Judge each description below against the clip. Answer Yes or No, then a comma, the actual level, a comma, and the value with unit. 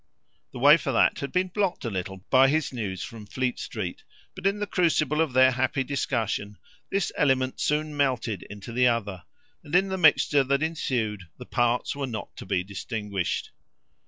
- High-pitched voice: No, low, 130 Hz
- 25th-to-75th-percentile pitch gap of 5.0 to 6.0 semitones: Yes, wide, 5.6 semitones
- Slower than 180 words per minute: No, average, 185 wpm